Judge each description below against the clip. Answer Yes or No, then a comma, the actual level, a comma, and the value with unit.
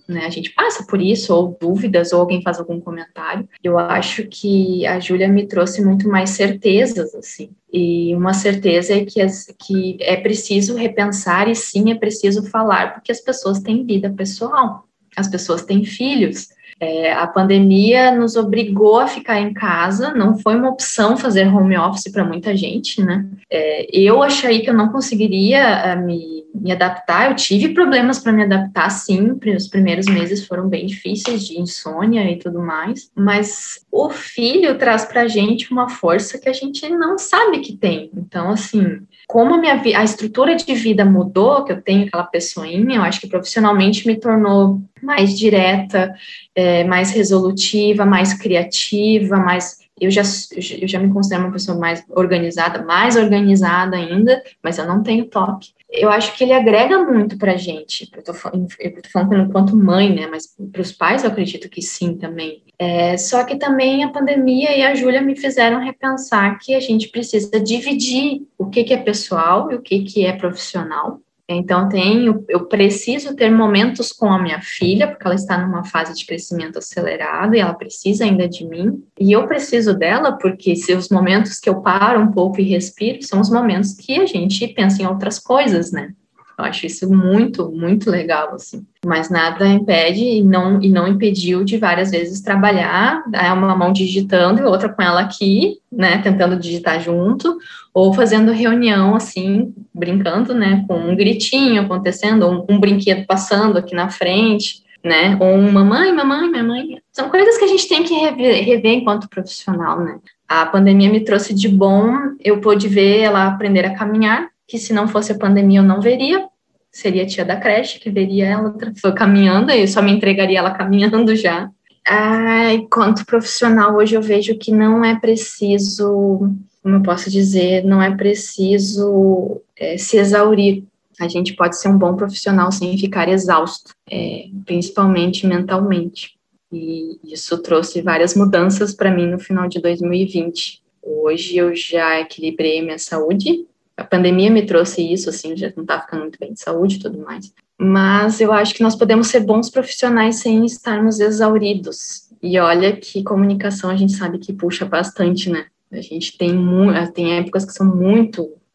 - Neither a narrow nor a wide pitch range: Yes, average, 3.3 semitones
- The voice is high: Yes, high, 200 Hz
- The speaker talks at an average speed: Yes, average, 175 wpm